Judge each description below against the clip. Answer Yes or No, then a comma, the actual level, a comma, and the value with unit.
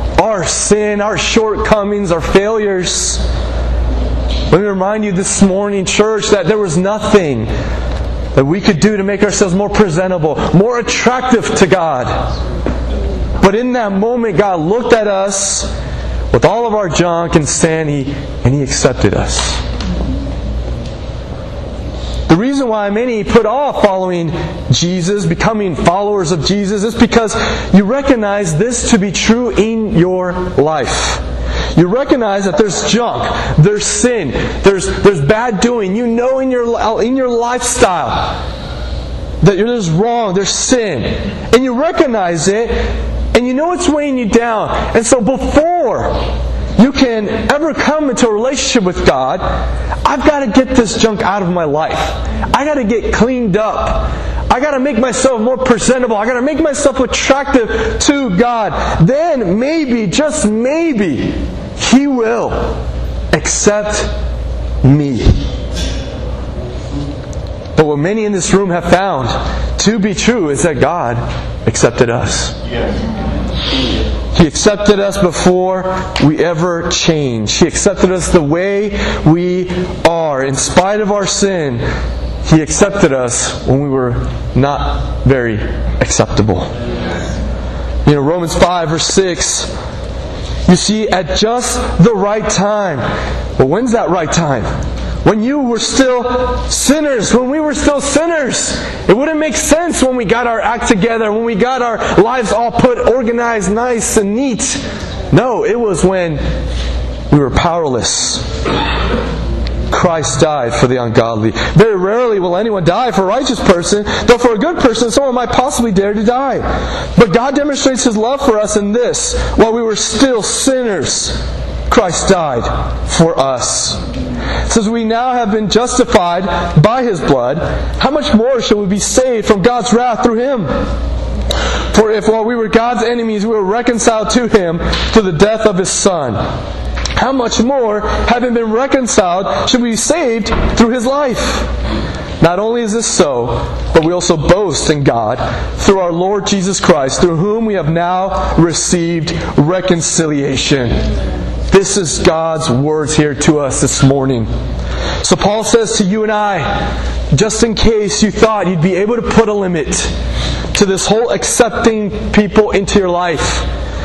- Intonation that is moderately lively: No, wide, 6.3 semitones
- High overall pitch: Yes, high, 205 Hz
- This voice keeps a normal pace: Yes, average, 150 wpm